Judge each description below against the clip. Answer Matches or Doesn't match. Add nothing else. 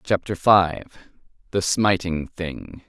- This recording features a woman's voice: Doesn't match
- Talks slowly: Matches